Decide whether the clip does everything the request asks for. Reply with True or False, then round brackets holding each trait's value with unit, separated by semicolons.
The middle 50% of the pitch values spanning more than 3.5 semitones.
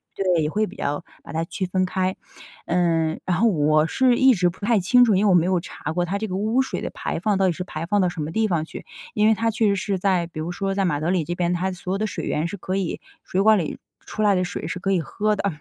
False (3.2 semitones)